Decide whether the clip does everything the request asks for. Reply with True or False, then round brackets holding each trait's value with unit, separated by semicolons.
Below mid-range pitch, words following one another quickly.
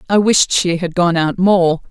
False (180 Hz; 220 wpm)